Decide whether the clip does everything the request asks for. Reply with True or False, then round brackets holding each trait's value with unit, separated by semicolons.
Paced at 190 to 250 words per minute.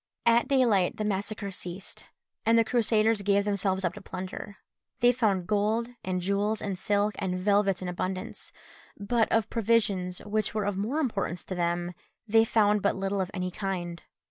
False (170 wpm)